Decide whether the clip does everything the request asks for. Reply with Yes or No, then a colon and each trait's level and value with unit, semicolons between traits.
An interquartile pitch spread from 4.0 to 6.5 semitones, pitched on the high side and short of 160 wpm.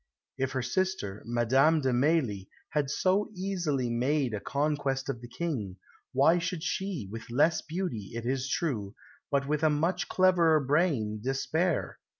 No: wide, 5.5 semitones; medium, 140 Hz; average, 150 wpm